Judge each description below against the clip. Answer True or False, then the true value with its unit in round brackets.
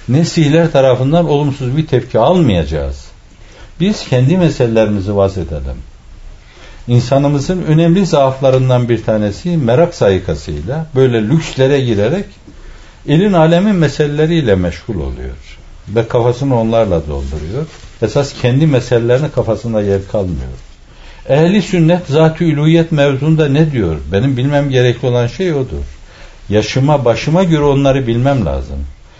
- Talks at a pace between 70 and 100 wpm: False (115 wpm)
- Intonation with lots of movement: True (7.6 semitones)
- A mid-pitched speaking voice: False (125 Hz)